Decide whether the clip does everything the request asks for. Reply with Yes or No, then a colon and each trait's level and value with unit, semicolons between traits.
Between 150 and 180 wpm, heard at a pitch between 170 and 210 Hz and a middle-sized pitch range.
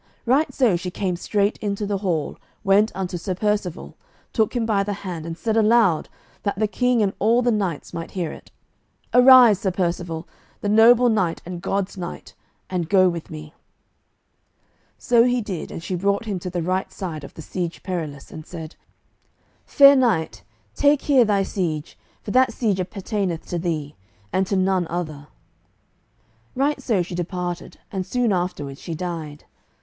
Yes: average, 170 wpm; high, 190 Hz; average, 4.0 semitones